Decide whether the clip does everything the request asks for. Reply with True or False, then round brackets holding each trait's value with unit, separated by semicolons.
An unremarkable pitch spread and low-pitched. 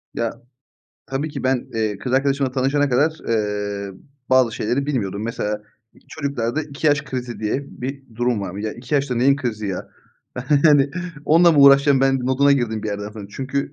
True (4.3 semitones; 130 Hz)